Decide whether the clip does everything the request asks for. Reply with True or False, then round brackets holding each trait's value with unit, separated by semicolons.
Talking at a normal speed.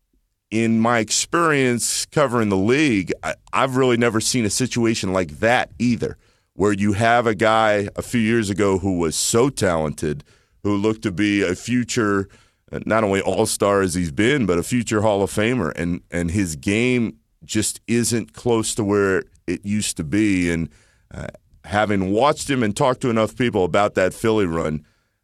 True (180 wpm)